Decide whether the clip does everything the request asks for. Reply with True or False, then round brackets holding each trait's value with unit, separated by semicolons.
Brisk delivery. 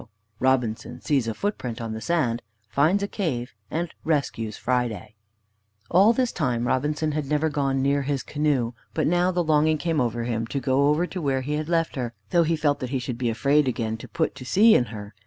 True (215 wpm)